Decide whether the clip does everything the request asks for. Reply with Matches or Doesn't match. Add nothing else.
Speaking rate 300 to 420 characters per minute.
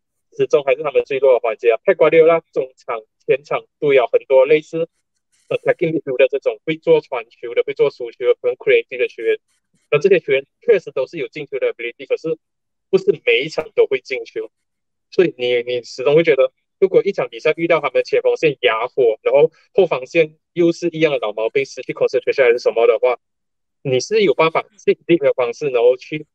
Matches